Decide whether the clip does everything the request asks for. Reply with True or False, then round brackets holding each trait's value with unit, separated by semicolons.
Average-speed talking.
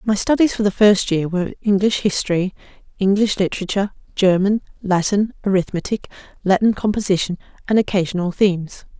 False (125 wpm)